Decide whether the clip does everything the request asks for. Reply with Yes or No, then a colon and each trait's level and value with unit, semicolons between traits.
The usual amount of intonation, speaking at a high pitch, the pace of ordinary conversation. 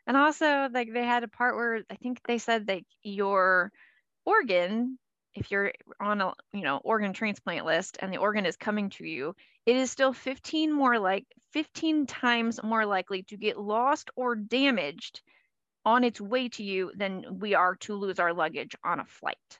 Yes: average, 4.1 semitones; high, 225 Hz; average, 185 wpm